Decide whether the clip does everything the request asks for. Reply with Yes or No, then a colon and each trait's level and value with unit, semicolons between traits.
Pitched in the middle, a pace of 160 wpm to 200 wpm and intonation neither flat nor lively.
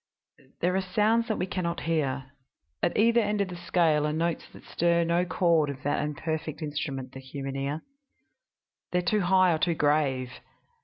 Yes: medium, 165 Hz; average, 190 wpm; average, 3.8 semitones